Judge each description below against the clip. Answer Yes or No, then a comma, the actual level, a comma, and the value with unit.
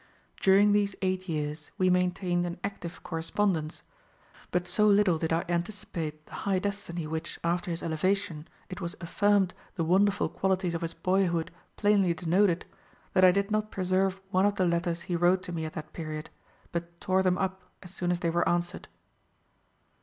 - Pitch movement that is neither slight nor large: No, narrow, 2.3 semitones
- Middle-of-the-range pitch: Yes, medium, 180 Hz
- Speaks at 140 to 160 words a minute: No, average, 175 wpm